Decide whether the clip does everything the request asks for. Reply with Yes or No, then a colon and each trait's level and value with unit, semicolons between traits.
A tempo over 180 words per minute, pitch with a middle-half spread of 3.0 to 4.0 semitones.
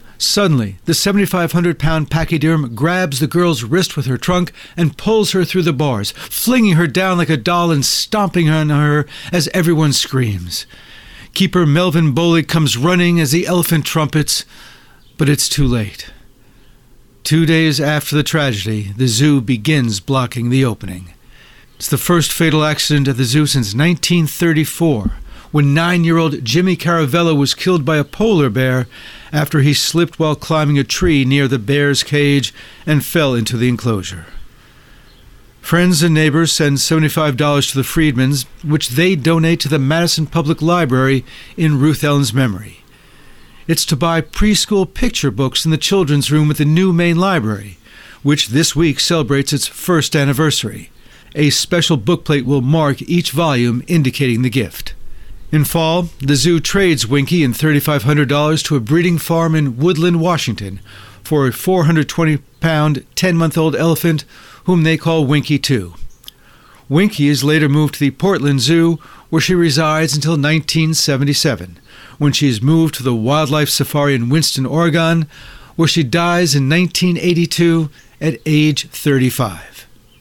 No: average, 155 wpm; average, 3.4 semitones